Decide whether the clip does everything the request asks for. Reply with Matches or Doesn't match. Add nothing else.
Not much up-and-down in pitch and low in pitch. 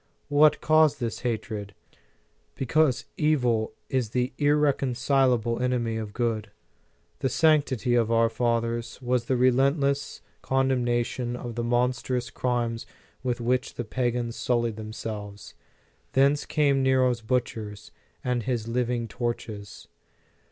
Matches